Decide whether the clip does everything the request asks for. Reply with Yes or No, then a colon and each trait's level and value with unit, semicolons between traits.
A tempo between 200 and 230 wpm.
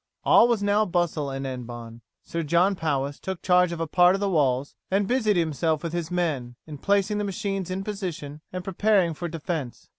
Yes: fast, 205 wpm